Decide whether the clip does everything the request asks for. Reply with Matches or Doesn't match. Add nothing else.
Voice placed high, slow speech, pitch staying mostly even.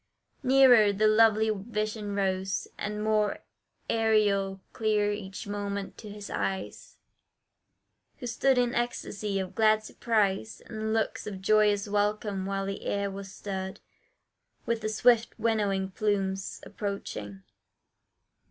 Matches